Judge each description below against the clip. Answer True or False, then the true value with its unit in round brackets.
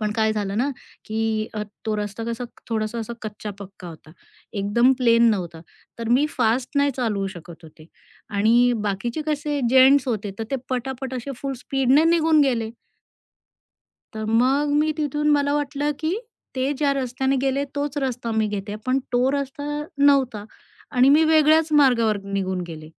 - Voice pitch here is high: True (245 Hz)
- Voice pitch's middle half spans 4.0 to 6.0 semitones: True (4.7 semitones)